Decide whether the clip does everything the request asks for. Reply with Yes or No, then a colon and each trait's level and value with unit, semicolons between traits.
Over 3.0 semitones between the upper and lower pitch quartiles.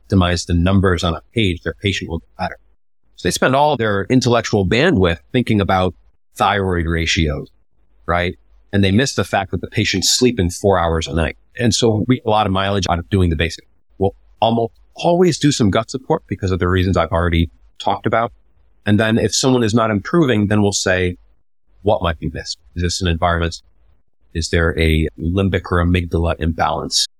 Yes: average, 4.2 semitones